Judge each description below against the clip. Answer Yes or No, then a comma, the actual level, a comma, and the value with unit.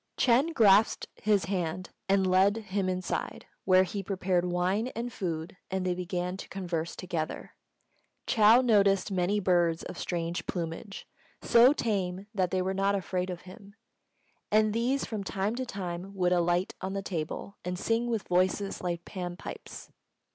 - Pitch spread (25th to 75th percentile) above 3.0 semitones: No, narrow, 2.4 semitones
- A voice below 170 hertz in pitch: No, high, 190 Hz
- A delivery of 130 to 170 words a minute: Yes, average, 160 wpm